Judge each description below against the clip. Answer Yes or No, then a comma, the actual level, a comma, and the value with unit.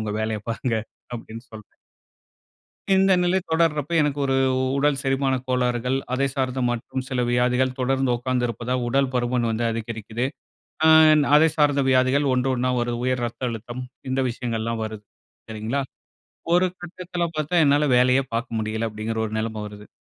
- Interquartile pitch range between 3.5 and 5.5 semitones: No, average, 3.1 semitones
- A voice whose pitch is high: No, low, 125 Hz